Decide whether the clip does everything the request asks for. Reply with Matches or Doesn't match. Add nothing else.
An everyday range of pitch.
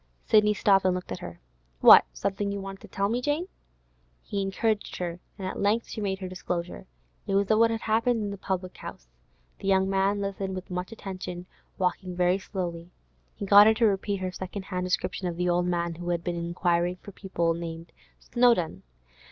Doesn't match